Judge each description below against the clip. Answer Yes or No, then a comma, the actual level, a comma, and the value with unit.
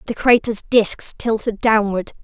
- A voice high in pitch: Yes, high, 220 Hz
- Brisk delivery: No, slow, 135 wpm